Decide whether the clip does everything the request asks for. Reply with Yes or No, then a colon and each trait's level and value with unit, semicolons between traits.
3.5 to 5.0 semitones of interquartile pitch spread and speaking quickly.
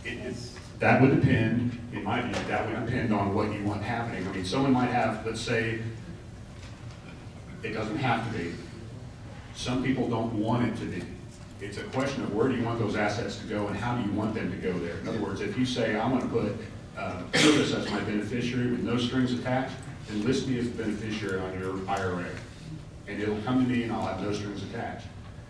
No: average, 2.8 semitones; fast, 225 wpm